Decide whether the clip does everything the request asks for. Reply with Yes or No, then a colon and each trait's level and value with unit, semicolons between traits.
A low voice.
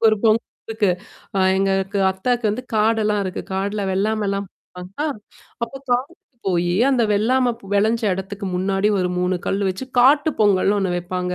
No: high, 200 Hz